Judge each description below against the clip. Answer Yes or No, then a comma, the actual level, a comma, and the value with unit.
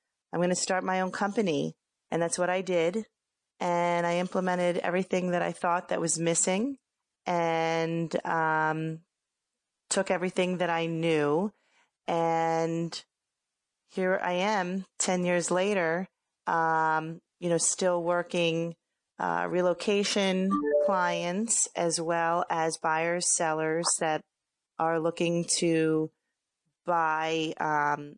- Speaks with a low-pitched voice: No, medium, 170 Hz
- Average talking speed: No, slow, 115 wpm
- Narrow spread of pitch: Yes, narrow, 1.9 semitones